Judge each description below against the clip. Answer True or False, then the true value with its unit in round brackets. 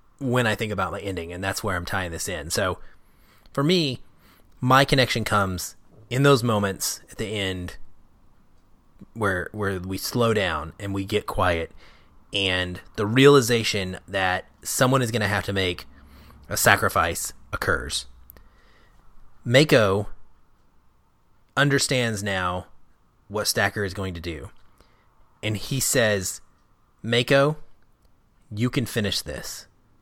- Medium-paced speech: False (130 wpm)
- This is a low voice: True (100 Hz)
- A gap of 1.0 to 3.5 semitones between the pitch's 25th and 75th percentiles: False (4.2 semitones)